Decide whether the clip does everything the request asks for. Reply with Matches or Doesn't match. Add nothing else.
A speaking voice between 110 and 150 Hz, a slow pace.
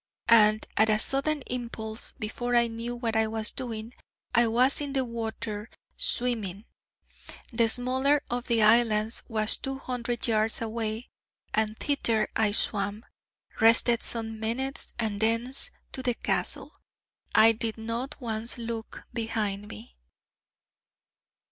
Doesn't match